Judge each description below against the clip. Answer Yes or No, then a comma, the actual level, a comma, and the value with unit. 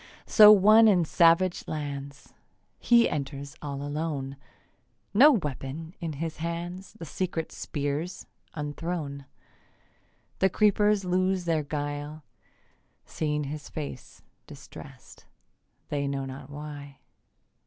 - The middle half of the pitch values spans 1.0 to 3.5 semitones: No, average, 4.0 semitones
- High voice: No, medium, 155 Hz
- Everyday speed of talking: No, slow, 105 wpm